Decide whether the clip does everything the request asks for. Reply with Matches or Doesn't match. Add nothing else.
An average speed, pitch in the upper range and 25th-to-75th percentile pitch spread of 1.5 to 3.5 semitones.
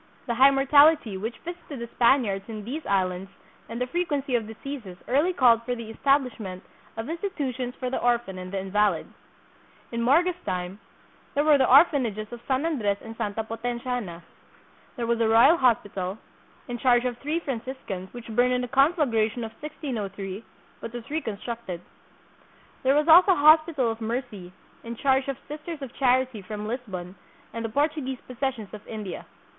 Doesn't match